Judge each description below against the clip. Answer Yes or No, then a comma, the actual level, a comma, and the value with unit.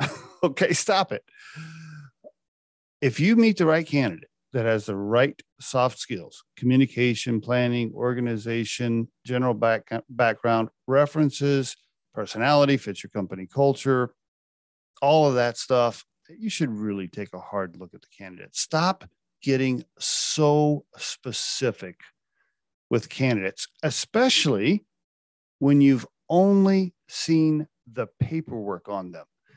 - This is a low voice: Yes, low, 125 Hz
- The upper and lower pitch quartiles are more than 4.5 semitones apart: Yes, average, 5.2 semitones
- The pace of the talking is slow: Yes, slow, 115 wpm